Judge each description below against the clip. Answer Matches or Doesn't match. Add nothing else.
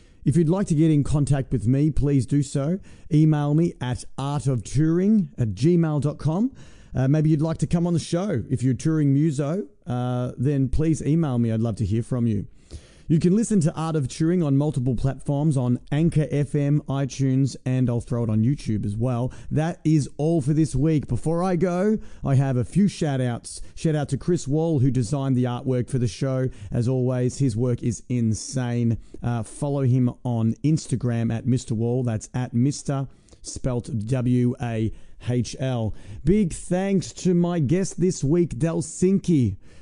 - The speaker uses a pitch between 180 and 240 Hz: Doesn't match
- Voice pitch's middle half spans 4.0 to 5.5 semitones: Matches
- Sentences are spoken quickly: Doesn't match